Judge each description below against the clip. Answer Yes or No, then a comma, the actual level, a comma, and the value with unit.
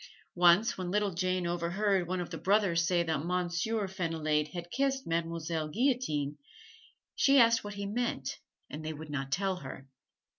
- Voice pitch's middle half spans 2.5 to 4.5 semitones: Yes, average, 3.8 semitones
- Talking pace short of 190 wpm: Yes, average, 160 wpm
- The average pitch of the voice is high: No, medium, 175 Hz